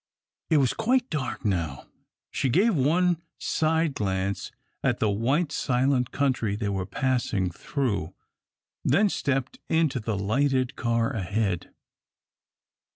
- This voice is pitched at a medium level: No, low, 130 Hz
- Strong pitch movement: Yes, wide, 6.5 semitones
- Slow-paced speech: Yes, slow, 120 wpm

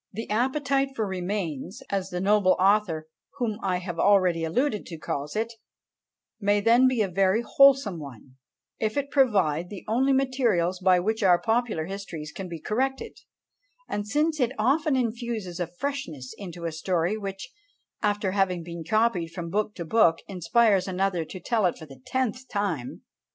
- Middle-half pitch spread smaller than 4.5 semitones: No, average, 5.0 semitones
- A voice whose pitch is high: Yes, high, 200 Hz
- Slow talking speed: No, average, 165 wpm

